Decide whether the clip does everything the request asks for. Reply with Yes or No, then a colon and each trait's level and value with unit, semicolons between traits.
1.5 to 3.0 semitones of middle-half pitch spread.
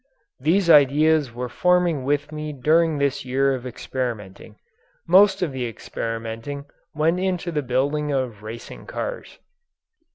No: average, 4.1 semitones